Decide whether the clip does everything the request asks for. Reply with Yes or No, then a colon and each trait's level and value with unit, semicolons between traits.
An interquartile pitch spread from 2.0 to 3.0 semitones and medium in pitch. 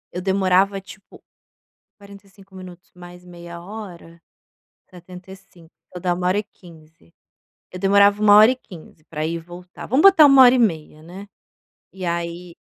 Yes: average, 2.7 semitones; medium, 180 Hz